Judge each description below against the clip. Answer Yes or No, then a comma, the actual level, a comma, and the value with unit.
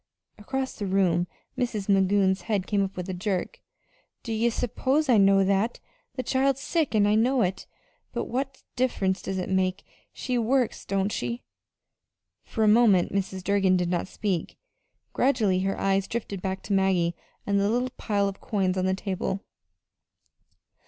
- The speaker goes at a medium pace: Yes, average, 165 wpm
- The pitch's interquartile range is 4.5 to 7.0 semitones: No, average, 3.7 semitones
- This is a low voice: No, high, 200 Hz